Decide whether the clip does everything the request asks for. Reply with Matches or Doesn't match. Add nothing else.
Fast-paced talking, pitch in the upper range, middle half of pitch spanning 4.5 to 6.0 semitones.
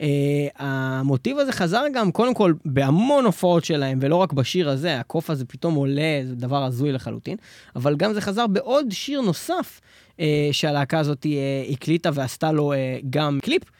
Doesn't match